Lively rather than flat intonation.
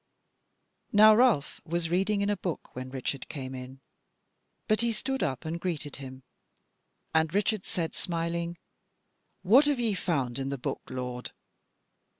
Yes: wide, 7.4 semitones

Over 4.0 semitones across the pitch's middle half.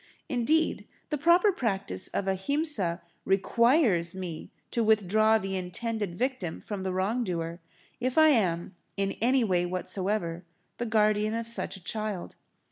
Yes: average, 4.5 semitones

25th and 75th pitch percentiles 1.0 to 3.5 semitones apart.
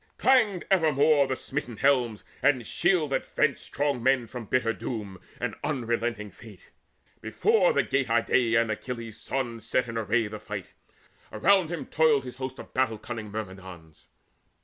No: average, 4.5 semitones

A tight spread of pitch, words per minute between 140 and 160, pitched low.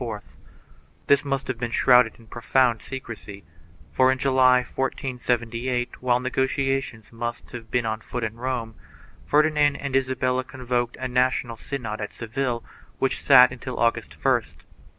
Yes: narrow, 2.0 semitones; average, 150 wpm; low, 125 Hz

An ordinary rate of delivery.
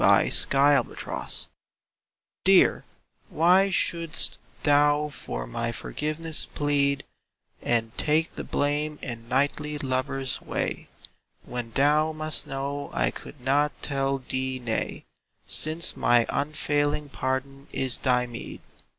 No: slow, 105 wpm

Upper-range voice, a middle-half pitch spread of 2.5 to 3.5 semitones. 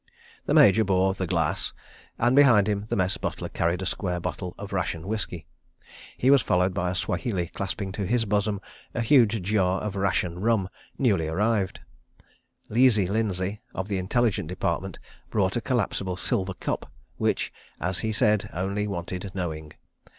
No: very low, 95 Hz; average, 2.9 semitones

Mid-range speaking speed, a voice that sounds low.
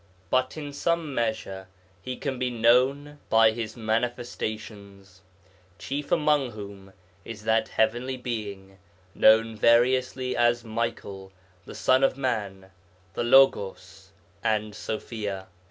No: slow, 115 wpm; low, 115 Hz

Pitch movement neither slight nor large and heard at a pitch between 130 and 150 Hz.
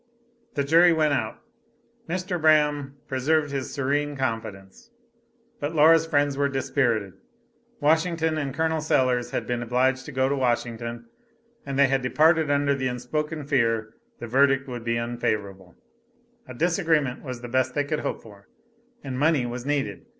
Yes: average, 3.8 semitones; low, 135 Hz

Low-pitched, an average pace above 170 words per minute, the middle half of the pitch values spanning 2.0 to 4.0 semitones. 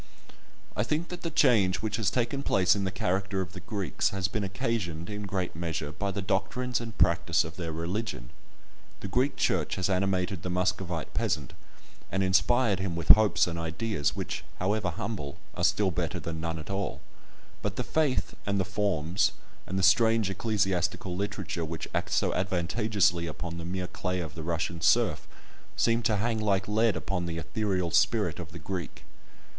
Yes: very low, 95 Hz; average, 180 wpm; average, 3.6 semitones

